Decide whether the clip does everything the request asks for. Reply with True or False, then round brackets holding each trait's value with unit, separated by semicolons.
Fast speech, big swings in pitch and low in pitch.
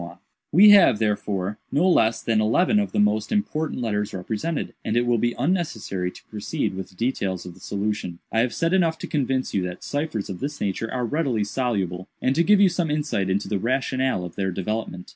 True (215 wpm; 6.9 semitones; 115 Hz)